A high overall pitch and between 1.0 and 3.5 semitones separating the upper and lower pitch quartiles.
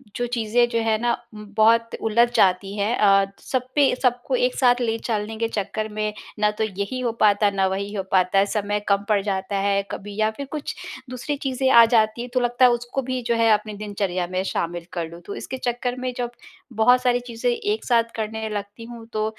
Yes: high, 220 Hz; average, 3.2 semitones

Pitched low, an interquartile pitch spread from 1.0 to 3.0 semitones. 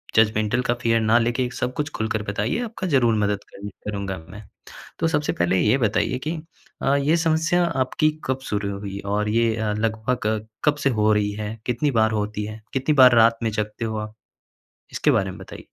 No: low, 110 Hz; average, 3.5 semitones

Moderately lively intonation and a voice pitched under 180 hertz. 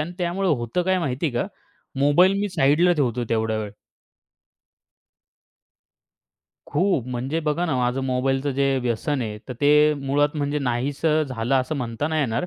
Yes: average, 4.0 semitones; medium, 140 Hz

